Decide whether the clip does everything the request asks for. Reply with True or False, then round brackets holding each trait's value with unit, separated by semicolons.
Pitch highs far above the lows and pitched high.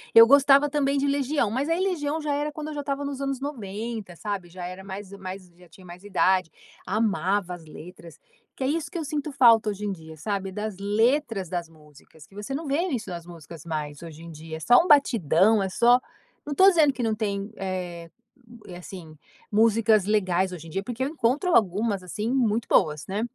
True (7.1 semitones; 210 Hz)